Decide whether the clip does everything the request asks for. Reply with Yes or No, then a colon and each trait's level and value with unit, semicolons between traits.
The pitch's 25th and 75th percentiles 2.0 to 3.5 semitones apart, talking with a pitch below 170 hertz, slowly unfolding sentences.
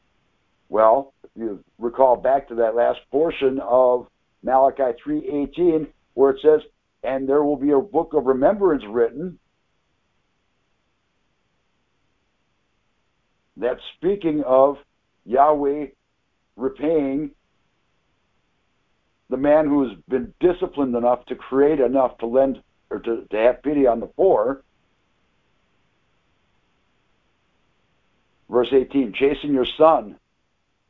Yes: average, 3.0 semitones; low, 135 Hz; slow, 105 wpm